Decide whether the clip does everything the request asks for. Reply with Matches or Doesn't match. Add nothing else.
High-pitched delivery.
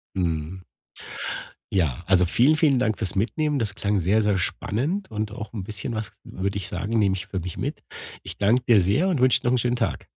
Doesn't match